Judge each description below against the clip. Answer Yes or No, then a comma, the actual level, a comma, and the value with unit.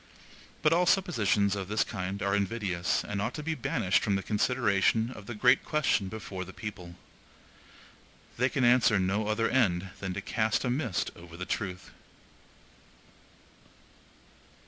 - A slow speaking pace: No, average, 150 wpm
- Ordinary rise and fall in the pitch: Yes, average, 4.2 semitones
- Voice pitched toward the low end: Yes, low, 105 Hz